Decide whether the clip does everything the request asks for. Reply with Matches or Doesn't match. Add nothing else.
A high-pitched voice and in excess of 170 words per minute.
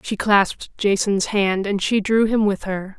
Matches